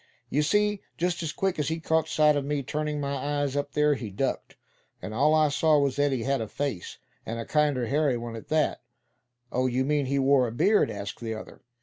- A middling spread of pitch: Yes, average, 3.0 semitones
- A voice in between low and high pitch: Yes, medium, 145 Hz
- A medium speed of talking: No, fast, 230 wpm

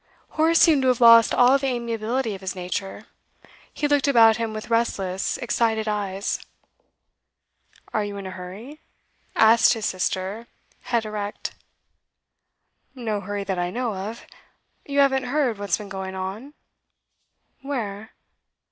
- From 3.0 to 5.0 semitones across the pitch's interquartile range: Yes, average, 3.9 semitones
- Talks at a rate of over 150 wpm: No, average, 140 wpm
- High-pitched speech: Yes, high, 220 Hz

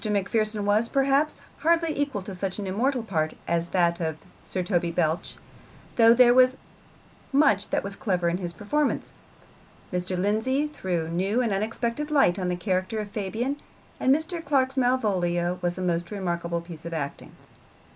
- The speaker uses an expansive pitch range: Yes, wide, 6.3 semitones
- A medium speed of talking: Yes, average, 165 wpm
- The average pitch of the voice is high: Yes, high, 205 Hz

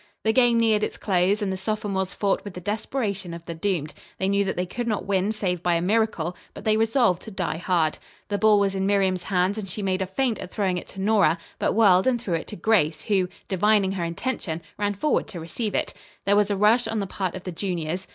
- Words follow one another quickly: Yes, fast, 245 wpm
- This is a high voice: Yes, high, 195 Hz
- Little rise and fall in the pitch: No, average, 3.0 semitones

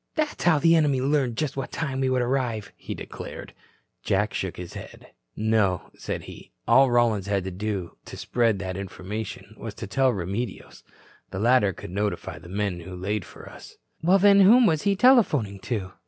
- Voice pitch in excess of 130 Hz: No, low, 110 Hz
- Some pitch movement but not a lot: No, wide, 6.1 semitones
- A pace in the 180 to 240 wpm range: Yes, average, 185 wpm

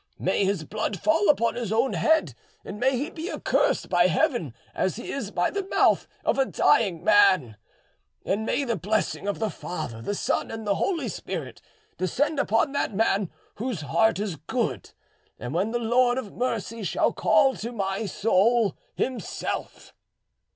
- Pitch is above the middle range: Yes, high, 220 Hz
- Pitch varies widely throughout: No, average, 4.3 semitones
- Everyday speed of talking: Yes, average, 165 wpm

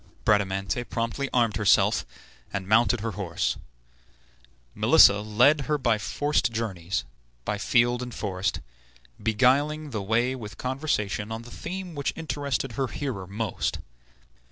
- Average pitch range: Yes, average, 4.4 semitones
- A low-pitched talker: Yes, low, 115 Hz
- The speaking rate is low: Yes, slow, 130 wpm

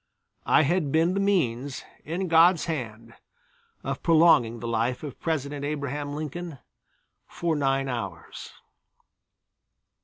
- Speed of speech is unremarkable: No, slow, 115 wpm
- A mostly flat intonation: No, average, 4.7 semitones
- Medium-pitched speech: Yes, medium, 145 Hz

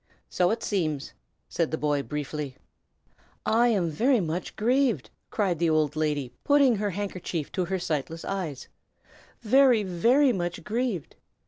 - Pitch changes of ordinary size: No, wide, 6.4 semitones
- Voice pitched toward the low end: No, medium, 180 Hz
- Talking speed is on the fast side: No, average, 140 wpm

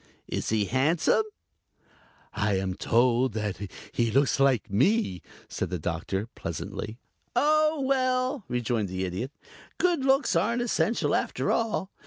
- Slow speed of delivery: Yes, slow, 125 wpm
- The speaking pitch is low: Yes, low, 125 Hz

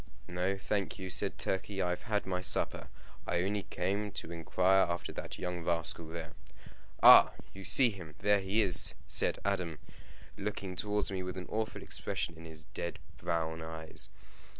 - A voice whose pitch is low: Yes, very low, 90 Hz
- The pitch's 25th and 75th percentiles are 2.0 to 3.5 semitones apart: Yes, average, 2.8 semitones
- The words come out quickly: No, average, 170 wpm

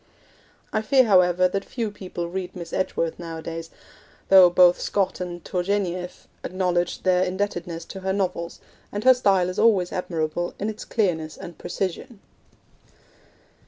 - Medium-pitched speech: Yes, medium, 180 Hz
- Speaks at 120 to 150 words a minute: Yes, average, 140 wpm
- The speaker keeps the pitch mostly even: Yes, narrow, 2.2 semitones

